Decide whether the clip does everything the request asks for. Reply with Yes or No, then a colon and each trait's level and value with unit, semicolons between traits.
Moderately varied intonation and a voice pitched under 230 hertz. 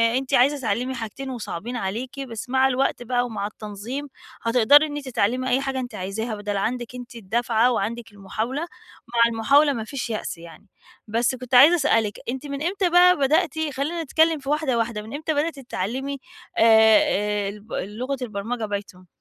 No: average, 4.1 semitones; high, 245 Hz